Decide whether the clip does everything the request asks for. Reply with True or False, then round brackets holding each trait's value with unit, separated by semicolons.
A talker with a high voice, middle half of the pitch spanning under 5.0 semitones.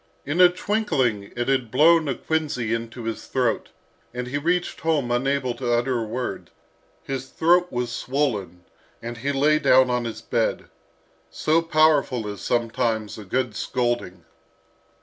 False (125 Hz; 4.1 semitones)